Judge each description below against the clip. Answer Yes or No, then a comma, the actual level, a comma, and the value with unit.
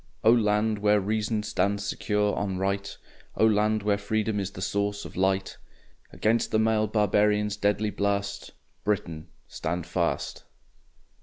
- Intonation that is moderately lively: No, narrow, 1.3 semitones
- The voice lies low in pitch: Yes, low, 105 Hz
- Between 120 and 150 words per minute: Yes, average, 140 wpm